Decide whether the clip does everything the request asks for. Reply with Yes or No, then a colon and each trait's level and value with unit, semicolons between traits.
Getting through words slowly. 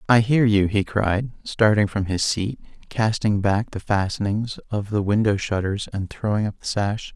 No: average, 185 wpm